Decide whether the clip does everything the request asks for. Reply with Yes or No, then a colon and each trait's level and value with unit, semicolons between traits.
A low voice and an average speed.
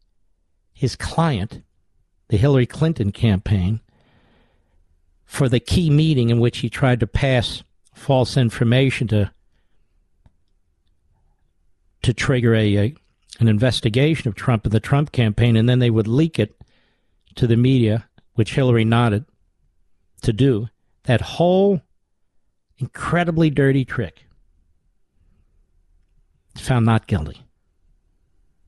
No: low, 110 Hz; slow, 110 wpm